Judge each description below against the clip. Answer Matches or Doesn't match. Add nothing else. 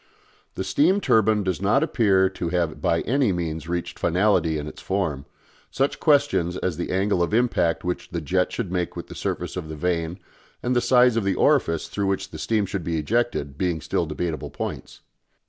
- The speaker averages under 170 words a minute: Doesn't match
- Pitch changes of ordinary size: Matches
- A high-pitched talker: Doesn't match